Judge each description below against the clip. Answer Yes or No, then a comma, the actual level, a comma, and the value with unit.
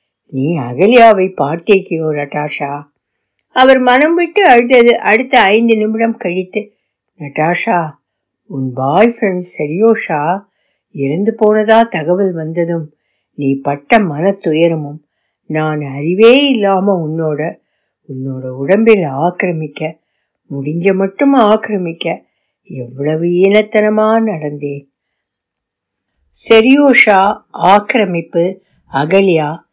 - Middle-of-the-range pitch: Yes, medium, 175 Hz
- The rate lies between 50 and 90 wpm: Yes, average, 80 wpm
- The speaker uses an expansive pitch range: Yes, wide, 6.6 semitones